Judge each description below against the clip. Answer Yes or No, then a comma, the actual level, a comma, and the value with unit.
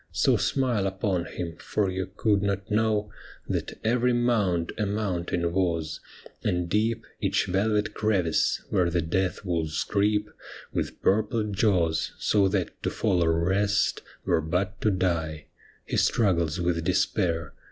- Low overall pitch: Yes, very low, 95 Hz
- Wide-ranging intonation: No, average, 3.6 semitones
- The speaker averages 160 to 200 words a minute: No, average, 150 wpm